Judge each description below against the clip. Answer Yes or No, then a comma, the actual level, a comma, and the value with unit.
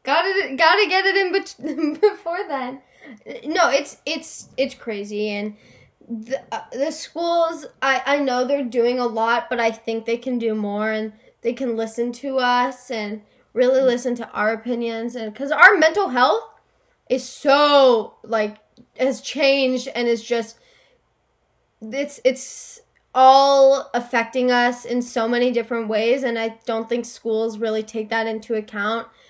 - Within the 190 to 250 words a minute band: No, average, 160 wpm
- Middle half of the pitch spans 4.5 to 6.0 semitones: No, average, 3.4 semitones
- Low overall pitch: No, high, 245 Hz